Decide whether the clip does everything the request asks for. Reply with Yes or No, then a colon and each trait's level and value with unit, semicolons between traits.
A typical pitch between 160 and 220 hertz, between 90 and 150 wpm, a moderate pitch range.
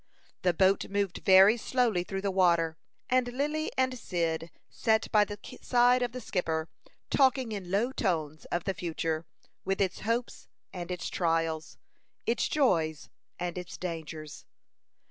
No: high, 190 Hz; average, 145 wpm; wide, 5.8 semitones